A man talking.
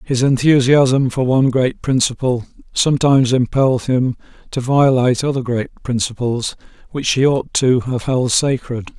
Yes: male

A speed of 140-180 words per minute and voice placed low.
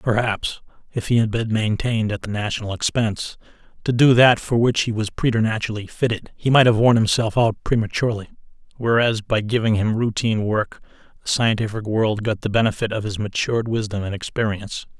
Yes: average, 175 wpm; low, 110 Hz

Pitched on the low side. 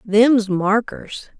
No: high, 215 Hz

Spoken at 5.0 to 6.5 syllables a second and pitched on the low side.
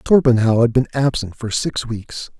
No: 4.5 syllables/s; low, 120 Hz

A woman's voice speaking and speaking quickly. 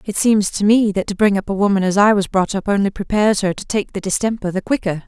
Yes: female; fast, 285 wpm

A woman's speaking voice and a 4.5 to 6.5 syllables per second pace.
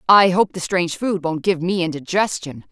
Yes: female; 5.2 syllables/s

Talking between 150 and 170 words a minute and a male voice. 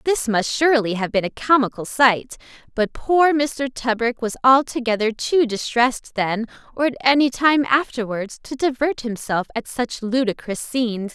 No: average, 155 wpm; female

